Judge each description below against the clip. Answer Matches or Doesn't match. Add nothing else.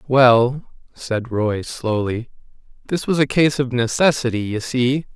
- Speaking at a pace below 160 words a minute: Matches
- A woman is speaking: Doesn't match